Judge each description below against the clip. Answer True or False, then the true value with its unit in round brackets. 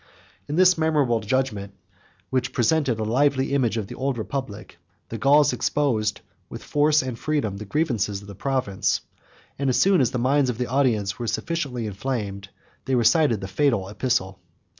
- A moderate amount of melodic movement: True (4.8 semitones)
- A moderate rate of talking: True (170 wpm)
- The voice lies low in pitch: True (125 Hz)